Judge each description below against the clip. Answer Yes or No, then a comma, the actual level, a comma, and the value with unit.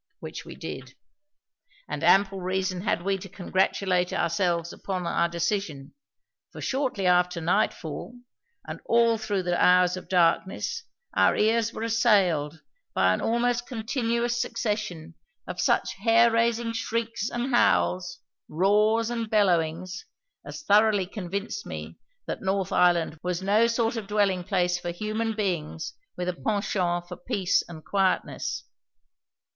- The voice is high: Yes, high, 195 Hz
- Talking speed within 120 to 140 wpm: Yes, slow, 135 wpm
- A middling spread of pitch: Yes, average, 4.2 semitones